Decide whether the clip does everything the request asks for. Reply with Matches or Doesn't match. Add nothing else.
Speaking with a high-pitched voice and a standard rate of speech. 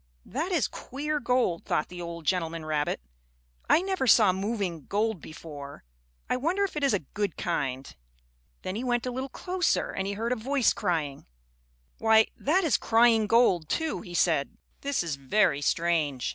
Matches